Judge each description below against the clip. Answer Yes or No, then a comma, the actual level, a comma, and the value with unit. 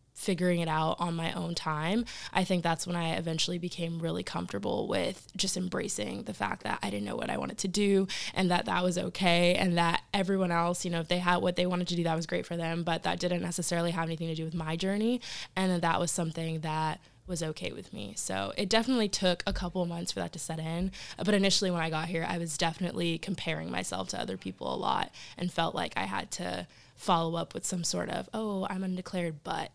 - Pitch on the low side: No, medium, 175 Hz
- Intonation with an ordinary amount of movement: No, narrow, 2.1 semitones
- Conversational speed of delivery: No, fast, 240 wpm